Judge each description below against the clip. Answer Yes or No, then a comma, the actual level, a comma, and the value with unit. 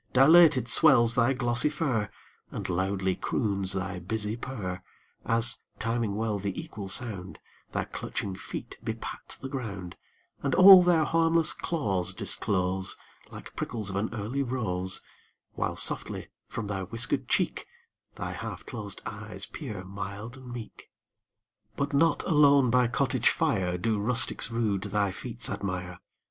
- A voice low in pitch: Yes, low, 115 Hz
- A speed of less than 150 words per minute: Yes, average, 140 wpm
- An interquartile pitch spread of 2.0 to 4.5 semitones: No, average, 5.0 semitones